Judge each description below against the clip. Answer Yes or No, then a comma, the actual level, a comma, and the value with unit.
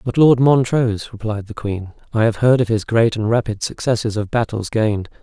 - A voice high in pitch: No, low, 115 Hz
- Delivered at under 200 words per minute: No, fast, 205 wpm